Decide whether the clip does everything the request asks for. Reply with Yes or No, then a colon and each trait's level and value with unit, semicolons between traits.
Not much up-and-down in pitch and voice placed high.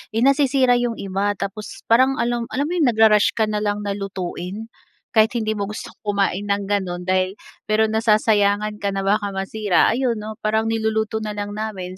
Yes: narrow, 1.9 semitones; high, 215 Hz